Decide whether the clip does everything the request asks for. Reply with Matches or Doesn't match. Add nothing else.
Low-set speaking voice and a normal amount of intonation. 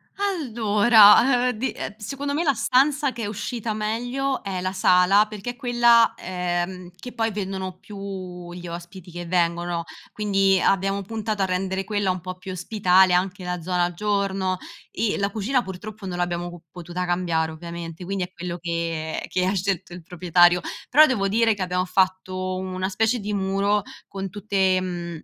Doesn't match